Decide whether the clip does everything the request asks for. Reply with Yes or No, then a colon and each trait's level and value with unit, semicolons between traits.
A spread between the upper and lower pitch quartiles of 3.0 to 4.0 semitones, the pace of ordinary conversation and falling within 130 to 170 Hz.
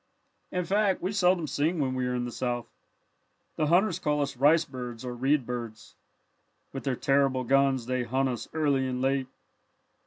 Yes: average, 3.4 semitones; average, 180 wpm; low, 135 Hz